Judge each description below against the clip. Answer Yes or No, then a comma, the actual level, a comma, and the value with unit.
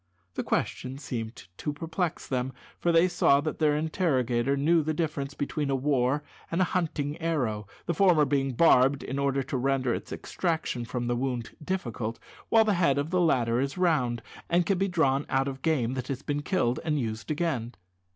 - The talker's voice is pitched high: No, medium, 140 Hz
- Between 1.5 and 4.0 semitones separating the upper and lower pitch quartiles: No, average, 4.4 semitones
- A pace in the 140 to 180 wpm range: No, average, 190 wpm